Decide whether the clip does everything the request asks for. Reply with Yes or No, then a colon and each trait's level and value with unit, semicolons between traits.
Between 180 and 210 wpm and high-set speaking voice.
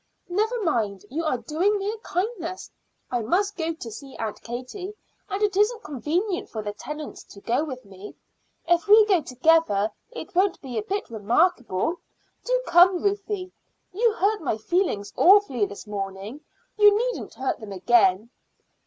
No: average, 160 wpm; very high, 325 Hz